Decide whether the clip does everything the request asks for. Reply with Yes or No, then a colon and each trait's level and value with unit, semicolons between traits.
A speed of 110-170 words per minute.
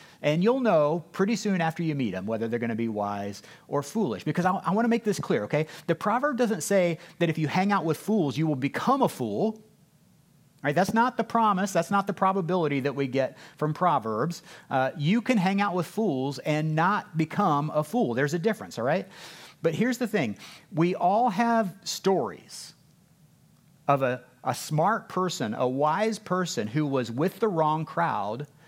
No: average, 200 wpm